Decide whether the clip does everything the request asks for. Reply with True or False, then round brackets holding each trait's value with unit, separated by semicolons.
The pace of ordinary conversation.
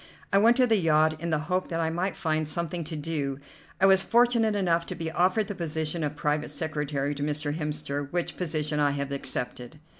False (210 wpm)